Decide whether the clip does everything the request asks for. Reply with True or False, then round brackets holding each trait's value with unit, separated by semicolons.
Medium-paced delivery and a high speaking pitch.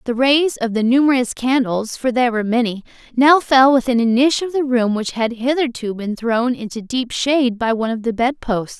False (220 wpm; 245 Hz)